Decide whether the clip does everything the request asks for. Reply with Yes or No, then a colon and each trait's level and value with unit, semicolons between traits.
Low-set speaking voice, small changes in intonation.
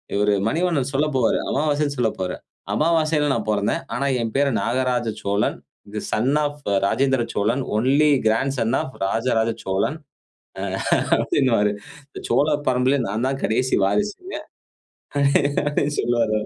No: low, 130 Hz; average, 4.5 semitones